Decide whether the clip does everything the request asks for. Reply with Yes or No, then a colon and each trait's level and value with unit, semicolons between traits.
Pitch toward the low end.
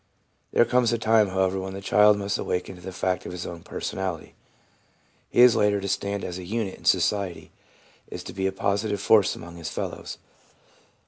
Yes: very low, 95 Hz